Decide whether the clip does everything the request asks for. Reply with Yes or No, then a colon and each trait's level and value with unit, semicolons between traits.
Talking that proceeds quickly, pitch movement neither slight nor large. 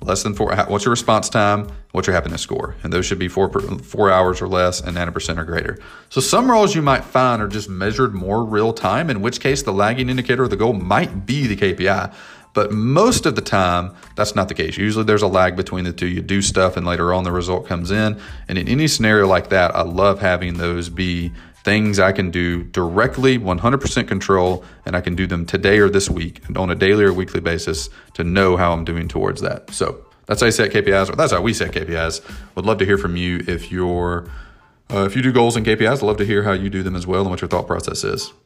Yes: fast, 250 wpm; average, 3.1 semitones